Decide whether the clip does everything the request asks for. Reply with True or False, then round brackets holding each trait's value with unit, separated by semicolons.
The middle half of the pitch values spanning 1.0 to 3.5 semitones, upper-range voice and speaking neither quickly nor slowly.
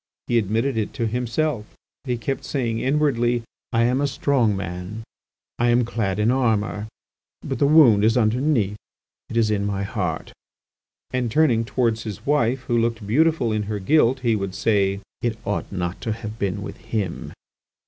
False (3.2 semitones; 115 Hz; 170 wpm)